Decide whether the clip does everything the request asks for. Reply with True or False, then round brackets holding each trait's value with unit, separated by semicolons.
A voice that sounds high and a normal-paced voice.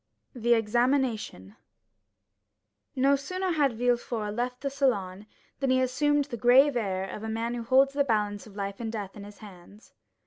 True (235 Hz; 170 wpm)